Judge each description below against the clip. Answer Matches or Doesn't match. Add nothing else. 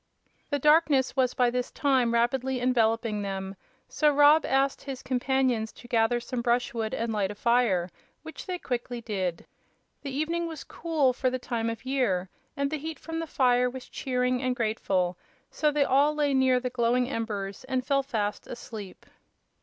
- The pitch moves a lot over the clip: Doesn't match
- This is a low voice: Doesn't match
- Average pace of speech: Matches